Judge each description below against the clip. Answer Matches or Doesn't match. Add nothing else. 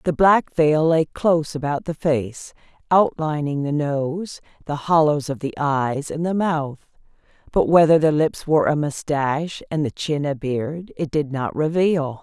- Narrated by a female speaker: Matches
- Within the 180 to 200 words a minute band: Doesn't match